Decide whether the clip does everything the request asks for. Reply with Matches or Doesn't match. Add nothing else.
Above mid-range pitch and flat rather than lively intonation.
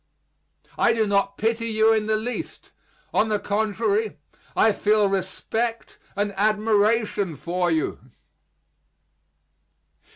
Matches